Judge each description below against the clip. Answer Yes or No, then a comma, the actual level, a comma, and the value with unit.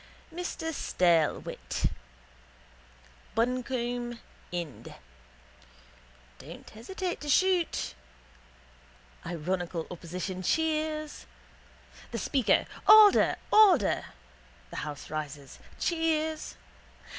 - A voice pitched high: Yes, high, 245 Hz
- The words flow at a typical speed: No, slow, 65 wpm